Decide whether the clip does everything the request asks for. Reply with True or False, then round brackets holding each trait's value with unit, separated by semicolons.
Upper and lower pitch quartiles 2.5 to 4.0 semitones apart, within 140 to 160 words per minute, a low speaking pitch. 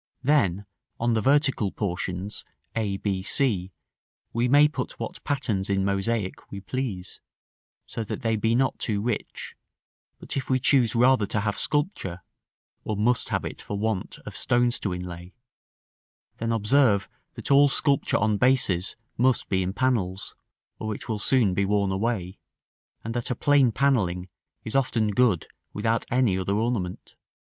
False (4.5 semitones; 155 wpm; 110 Hz)